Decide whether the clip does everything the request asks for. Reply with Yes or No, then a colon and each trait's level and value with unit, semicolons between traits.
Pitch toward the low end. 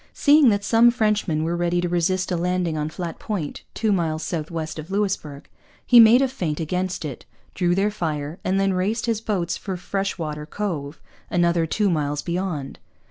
No: medium, 175 Hz